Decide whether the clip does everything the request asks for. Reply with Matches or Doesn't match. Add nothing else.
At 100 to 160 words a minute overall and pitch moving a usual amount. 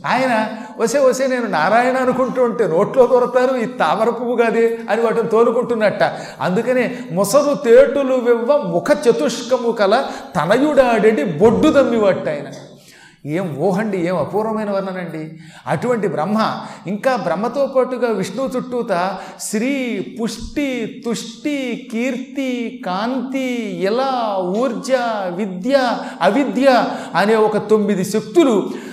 Matches